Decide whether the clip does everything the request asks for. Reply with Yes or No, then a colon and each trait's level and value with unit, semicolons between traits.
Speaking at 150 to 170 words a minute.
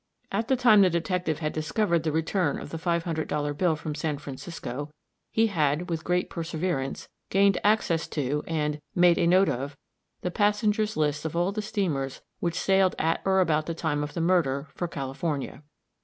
No: average, 185 wpm